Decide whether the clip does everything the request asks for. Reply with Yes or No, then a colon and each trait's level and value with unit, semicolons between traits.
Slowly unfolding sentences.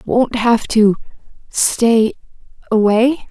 Yes: slow, 55 wpm